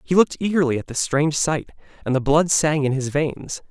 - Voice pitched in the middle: Yes, medium, 150 Hz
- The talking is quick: Yes, fast, 225 wpm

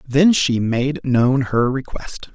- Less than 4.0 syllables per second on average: Yes, 3.2 syllables/s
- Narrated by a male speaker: Yes, male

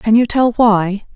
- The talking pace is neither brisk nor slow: No, fast, 210 wpm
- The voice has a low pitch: No, high, 220 Hz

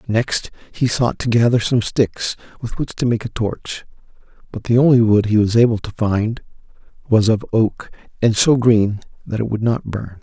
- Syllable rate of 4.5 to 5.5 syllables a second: Yes, 4.7 syllables/s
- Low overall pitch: Yes, low, 115 Hz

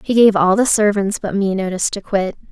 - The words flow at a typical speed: No, fast, 240 wpm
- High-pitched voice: Yes, high, 200 Hz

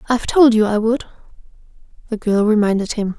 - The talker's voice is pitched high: Yes, high, 220 Hz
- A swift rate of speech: No, average, 170 wpm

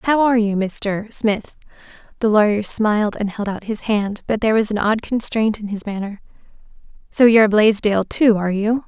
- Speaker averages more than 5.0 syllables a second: Yes, 5.2 syllables/s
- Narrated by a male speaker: No, female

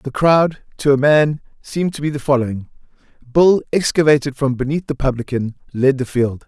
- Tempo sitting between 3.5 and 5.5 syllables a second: Yes, 5.2 syllables/s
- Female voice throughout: No, male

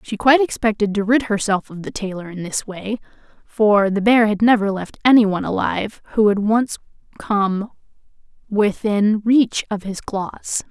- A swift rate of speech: No, average, 160 wpm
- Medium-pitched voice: No, high, 210 Hz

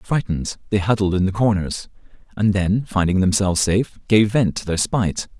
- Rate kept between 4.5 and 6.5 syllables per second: Yes, 5.5 syllables/s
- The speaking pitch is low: Yes, low, 100 Hz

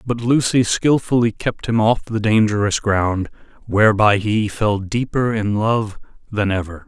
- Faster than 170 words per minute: No, average, 150 wpm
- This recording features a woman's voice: No, male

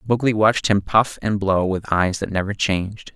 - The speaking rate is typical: No, fast, 210 wpm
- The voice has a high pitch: No, low, 100 Hz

